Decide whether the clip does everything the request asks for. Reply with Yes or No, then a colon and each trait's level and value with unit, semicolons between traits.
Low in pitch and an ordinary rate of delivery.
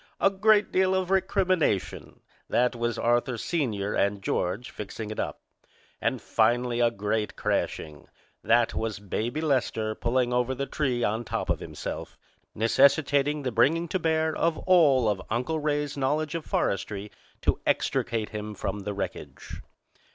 Yes: low, 125 Hz; average, 150 wpm